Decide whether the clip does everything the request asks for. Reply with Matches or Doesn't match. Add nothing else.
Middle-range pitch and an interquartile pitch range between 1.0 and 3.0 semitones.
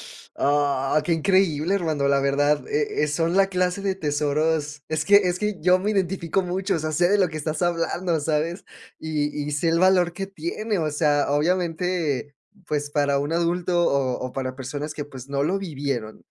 Doesn't match